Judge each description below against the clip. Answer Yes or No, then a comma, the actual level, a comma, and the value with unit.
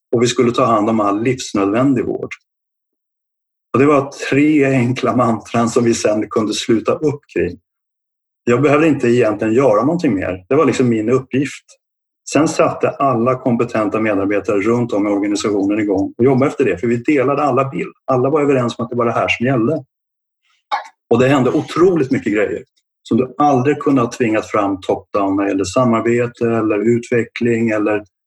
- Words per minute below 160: No, average, 175 wpm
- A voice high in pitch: No, low, 120 Hz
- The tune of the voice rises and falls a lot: No, average, 3.0 semitones